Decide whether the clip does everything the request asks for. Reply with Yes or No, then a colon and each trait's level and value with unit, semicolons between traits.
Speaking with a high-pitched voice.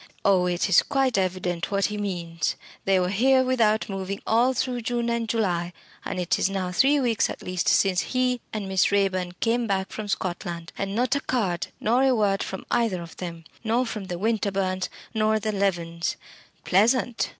Yes: high, 200 Hz